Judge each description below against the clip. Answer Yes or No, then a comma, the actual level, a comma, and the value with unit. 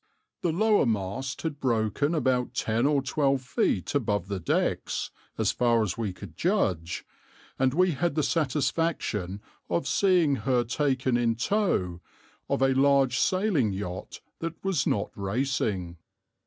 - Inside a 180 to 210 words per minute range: No, average, 140 wpm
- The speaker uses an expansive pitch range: Yes, wide, 6.3 semitones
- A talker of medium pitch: No, low, 130 Hz